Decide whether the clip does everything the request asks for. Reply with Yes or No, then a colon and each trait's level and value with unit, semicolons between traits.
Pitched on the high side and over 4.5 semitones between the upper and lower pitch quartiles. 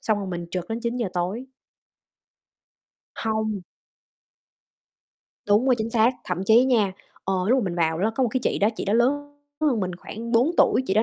No: high, 220 Hz; average, 3.8 semitones